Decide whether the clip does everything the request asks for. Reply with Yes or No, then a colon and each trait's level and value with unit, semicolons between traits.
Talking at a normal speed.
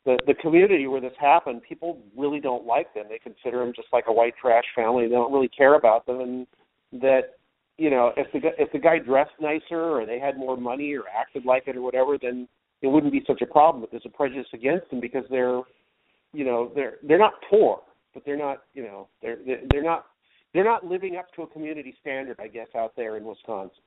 No: fast, 230 wpm